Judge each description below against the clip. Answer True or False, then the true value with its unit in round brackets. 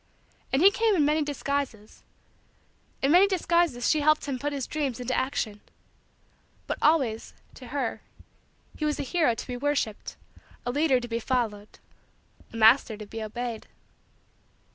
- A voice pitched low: False (265 Hz)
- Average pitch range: True (4.6 semitones)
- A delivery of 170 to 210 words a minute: False (155 wpm)